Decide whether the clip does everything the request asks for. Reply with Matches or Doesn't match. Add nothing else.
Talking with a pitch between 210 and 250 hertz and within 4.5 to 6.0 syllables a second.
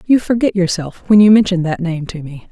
Doesn't match